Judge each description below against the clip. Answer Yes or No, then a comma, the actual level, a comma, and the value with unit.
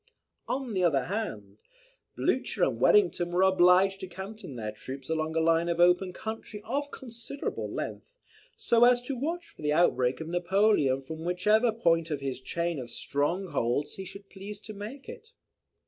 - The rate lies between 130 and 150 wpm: No, average, 170 wpm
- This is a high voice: No, medium, 180 Hz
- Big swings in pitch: Yes, wide, 5.8 semitones